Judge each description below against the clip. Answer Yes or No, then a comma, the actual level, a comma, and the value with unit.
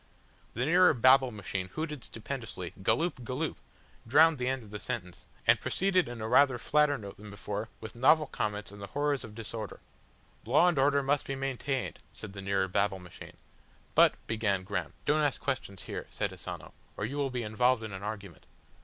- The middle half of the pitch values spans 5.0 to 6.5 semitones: Yes, wide, 5.4 semitones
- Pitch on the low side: Yes, low, 120 Hz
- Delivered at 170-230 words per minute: Yes, average, 190 wpm